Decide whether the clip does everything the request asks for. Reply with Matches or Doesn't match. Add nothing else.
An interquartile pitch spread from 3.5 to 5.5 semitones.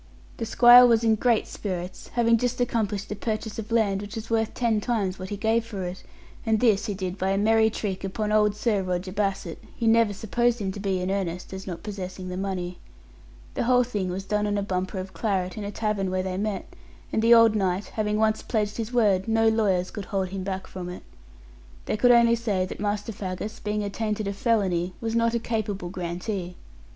Doesn't match